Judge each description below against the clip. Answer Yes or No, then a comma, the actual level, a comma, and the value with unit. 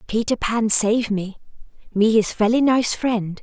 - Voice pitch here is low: No, high, 220 Hz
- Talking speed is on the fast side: No, average, 160 wpm